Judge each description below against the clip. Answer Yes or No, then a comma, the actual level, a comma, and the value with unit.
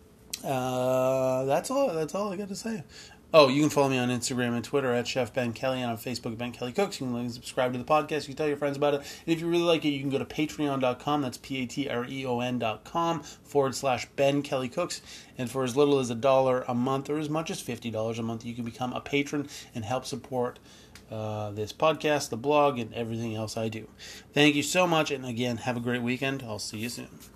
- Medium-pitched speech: No, low, 130 Hz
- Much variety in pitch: No, average, 3.3 semitones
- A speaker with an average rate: No, fast, 245 wpm